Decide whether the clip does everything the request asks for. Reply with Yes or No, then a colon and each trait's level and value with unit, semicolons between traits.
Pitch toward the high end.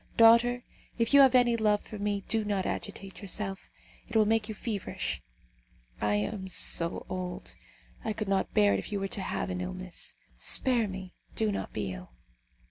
Yes: high, 200 Hz